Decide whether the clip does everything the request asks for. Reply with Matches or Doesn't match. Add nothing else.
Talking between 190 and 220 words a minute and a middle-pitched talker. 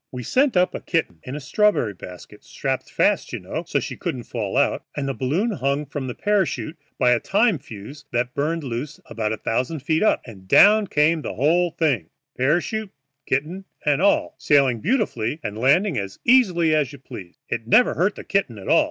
Matches